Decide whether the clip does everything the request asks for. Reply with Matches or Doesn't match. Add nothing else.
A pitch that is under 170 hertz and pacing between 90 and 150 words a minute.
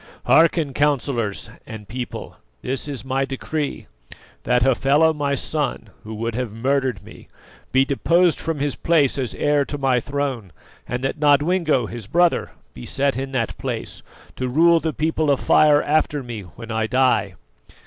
Doesn't match